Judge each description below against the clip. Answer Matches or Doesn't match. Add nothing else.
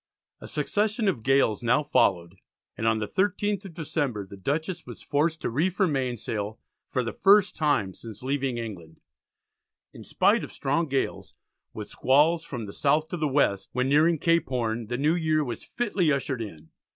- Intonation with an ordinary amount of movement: Doesn't match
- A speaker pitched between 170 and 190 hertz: Doesn't match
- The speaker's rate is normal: Matches